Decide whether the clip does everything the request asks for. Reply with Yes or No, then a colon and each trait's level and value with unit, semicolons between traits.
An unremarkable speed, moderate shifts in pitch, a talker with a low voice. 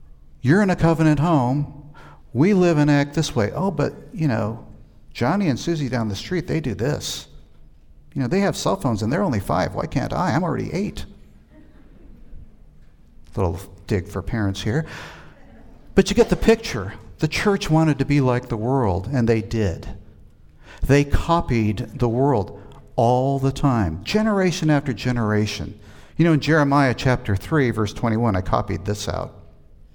No: average, 170 wpm; wide, 6.5 semitones; low, 120 Hz